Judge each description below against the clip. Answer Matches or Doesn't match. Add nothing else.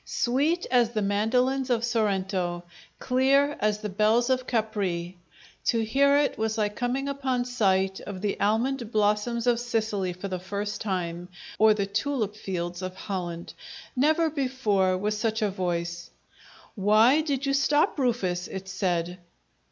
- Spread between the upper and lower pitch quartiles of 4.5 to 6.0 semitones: Matches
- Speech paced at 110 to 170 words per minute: Matches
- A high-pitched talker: Matches